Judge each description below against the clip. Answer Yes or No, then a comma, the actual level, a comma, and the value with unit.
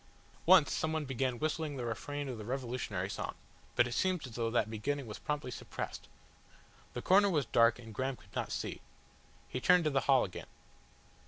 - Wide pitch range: No, average, 4.1 semitones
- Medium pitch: No, low, 130 Hz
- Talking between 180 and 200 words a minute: Yes, average, 185 wpm